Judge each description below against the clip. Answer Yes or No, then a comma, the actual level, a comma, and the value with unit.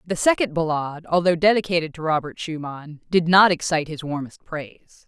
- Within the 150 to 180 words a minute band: Yes, average, 165 wpm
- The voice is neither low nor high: Yes, medium, 165 Hz